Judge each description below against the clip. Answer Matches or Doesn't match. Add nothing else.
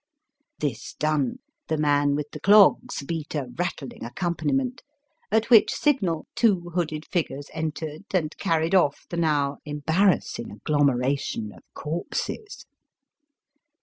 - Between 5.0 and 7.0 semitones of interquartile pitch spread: Doesn't match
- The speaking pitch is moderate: Matches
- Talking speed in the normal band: Doesn't match